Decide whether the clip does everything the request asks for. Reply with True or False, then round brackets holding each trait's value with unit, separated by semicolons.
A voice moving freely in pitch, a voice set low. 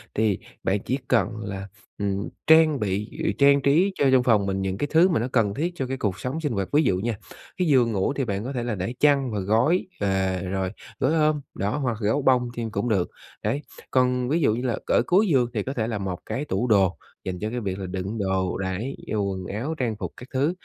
True (5.9 semitones; 115 Hz)